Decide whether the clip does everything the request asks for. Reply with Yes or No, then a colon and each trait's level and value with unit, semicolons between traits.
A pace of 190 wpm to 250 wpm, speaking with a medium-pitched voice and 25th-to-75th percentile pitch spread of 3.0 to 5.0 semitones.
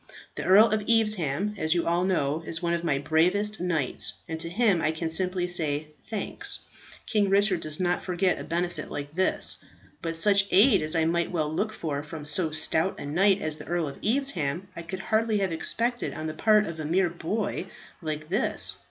Yes: fast, 205 wpm; medium, 175 Hz; average, 4.0 semitones